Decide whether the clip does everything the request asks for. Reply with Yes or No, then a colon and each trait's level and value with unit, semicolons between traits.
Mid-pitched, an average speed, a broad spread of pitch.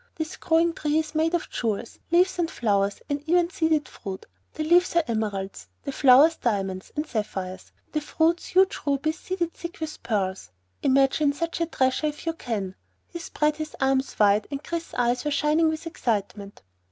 No: very high, 295 Hz; average, 175 wpm; wide, 6.8 semitones